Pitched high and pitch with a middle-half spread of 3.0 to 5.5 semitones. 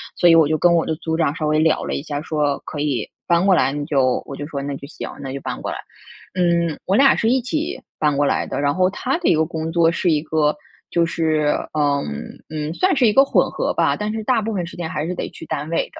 No: medium, 160 Hz; average, 3.3 semitones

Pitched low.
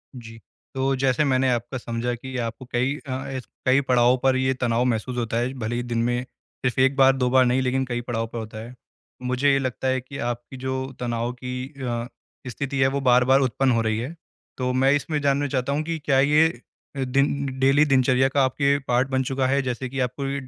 Yes: low, 130 Hz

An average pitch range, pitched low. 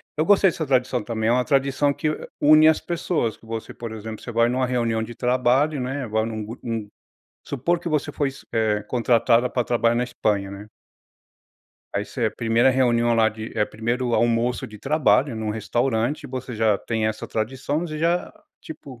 Yes: average, 3.5 semitones; low, 120 Hz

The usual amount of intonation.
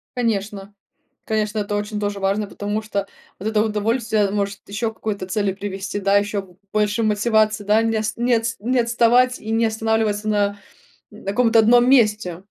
No: narrow, 1.7 semitones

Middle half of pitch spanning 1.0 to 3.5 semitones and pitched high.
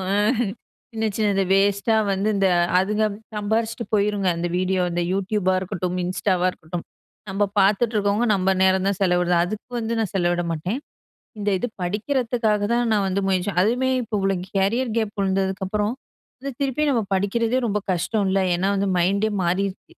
Yes: average, 2.7 semitones; high, 200 Hz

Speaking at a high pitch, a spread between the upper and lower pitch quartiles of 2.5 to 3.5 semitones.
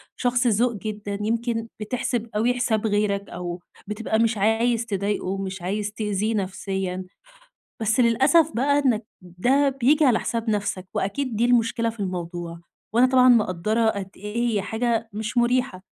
Yes: high, 220 Hz; average, 3.2 semitones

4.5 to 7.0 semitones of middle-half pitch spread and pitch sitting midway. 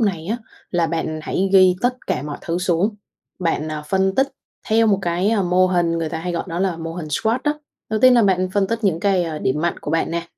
No: average, 3.2 semitones; medium, 180 Hz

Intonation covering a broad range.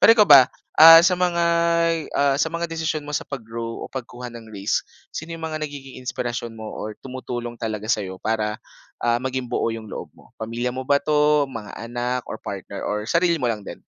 Yes: wide, 5.7 semitones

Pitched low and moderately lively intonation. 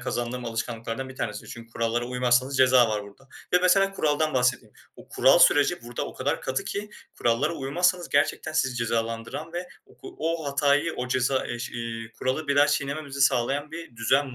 Yes: low, 130 Hz; average, 3.7 semitones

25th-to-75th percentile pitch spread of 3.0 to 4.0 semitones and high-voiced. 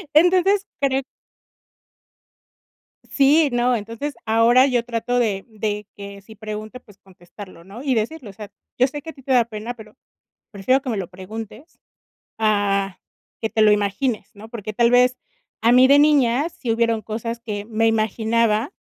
Yes: average, 3.3 semitones; high, 230 Hz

